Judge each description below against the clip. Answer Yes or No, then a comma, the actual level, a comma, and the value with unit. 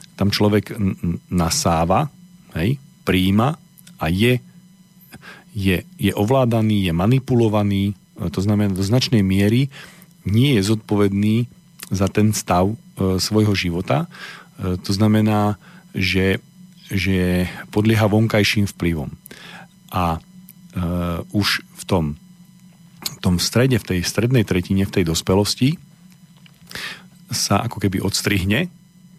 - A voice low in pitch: Yes, low, 105 Hz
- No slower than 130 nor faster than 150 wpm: No, average, 115 wpm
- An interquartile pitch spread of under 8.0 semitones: No, wide, 9.0 semitones